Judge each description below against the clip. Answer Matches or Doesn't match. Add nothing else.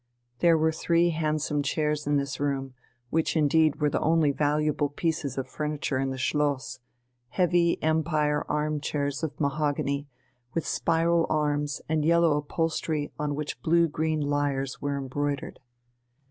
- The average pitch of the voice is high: Doesn't match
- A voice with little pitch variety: Matches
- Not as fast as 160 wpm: Matches